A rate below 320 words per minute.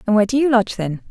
No: fast, 325 wpm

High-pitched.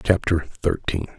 No: very low, 85 Hz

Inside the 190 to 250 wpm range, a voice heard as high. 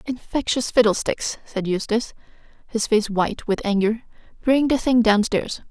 No: slow, 135 wpm; high, 225 Hz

